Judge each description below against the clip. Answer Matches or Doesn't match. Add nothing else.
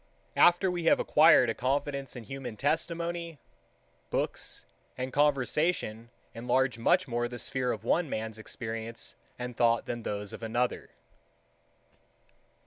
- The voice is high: Doesn't match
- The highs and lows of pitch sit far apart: Doesn't match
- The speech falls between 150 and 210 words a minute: Doesn't match